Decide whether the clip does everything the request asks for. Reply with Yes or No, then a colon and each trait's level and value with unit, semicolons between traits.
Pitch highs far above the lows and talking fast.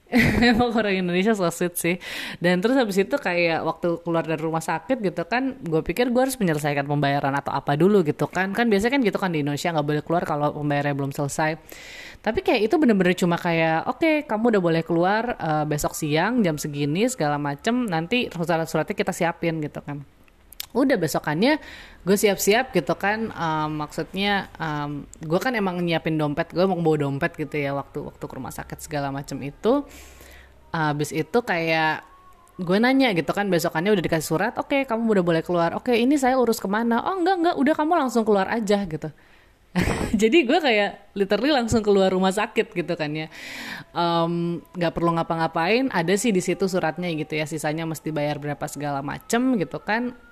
Yes: wide, 6.2 semitones; fast, 190 wpm